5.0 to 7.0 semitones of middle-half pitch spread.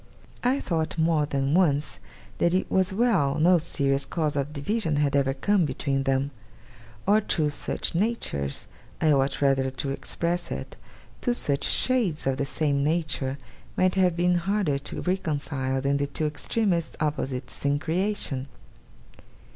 No: average, 4.4 semitones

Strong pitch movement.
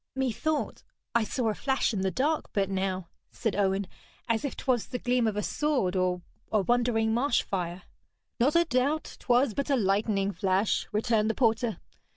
No: average, 4.6 semitones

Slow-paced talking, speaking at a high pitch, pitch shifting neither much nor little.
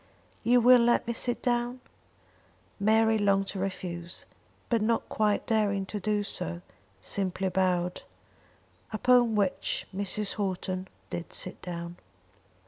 Yes: slow, 125 wpm; high, 200 Hz; average, 3.3 semitones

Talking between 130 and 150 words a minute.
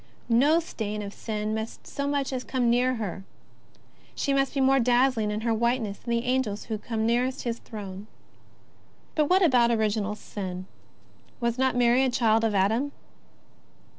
No: average, 165 wpm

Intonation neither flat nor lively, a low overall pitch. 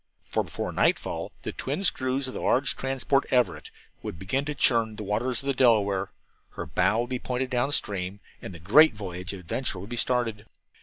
Yes: average, 4.4 semitones; low, 120 Hz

